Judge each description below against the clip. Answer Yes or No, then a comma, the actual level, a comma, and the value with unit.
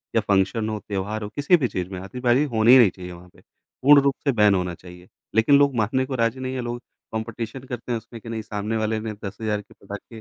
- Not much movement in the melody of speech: No, average, 3.6 semitones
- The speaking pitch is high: No, low, 110 Hz